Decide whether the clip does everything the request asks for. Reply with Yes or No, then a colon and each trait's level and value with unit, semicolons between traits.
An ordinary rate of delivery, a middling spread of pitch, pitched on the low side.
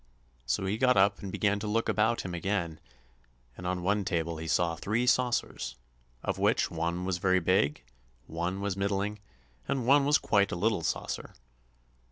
Yes: average, 175 wpm; average, 3.5 semitones; very low, 95 Hz